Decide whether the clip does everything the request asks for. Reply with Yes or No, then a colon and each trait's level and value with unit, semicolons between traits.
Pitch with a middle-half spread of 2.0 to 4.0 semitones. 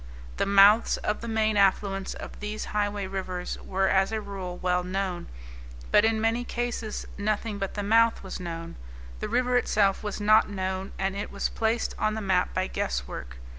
Yes: narrow, 2.4 semitones